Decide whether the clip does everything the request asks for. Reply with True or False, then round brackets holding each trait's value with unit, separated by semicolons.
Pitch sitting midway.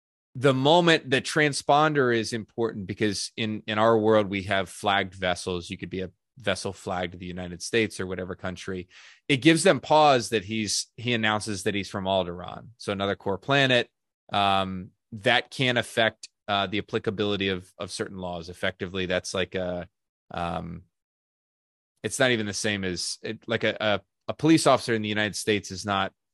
False (105 Hz)